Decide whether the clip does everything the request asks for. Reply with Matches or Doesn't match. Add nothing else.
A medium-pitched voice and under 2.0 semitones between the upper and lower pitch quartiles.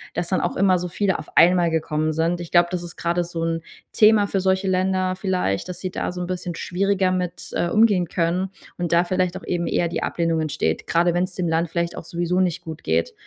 Matches